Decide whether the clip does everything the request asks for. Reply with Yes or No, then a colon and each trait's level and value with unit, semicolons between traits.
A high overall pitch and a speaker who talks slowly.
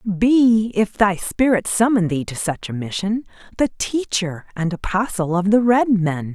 No: high, 205 Hz; average, 170 wpm